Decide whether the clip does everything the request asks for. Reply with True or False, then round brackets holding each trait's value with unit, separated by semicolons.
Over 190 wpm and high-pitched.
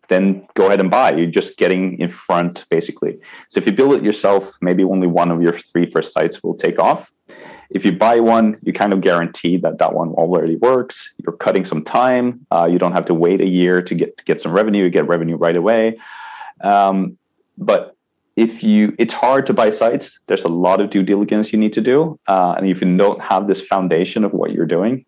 False (225 wpm; 95 Hz)